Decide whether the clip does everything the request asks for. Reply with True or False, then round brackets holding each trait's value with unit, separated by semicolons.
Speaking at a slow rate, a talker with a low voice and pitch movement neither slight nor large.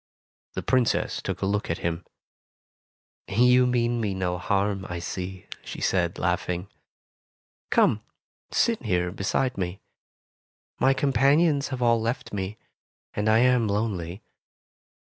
True (125 wpm; 105 Hz; 4.9 semitones)